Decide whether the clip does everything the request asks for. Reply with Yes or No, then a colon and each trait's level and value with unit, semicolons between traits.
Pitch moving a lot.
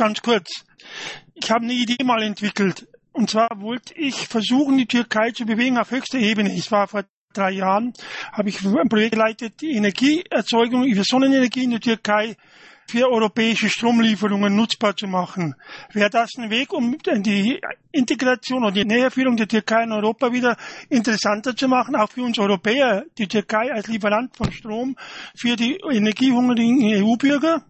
No: average, 3.1 semitones